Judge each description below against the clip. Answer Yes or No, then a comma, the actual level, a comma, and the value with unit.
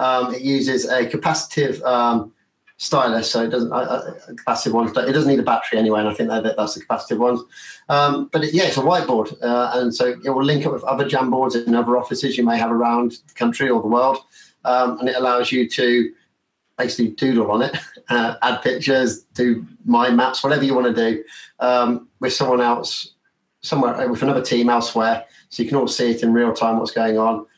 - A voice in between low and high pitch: No, low, 125 Hz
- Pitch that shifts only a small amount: Yes, narrow, 2.0 semitones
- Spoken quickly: Yes, fast, 215 wpm